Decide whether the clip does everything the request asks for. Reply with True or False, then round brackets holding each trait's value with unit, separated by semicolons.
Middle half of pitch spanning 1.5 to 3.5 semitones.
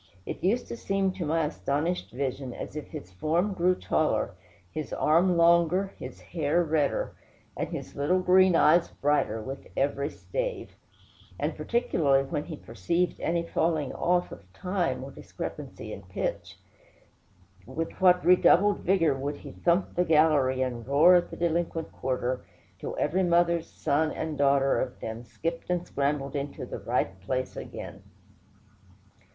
False (4.3 semitones)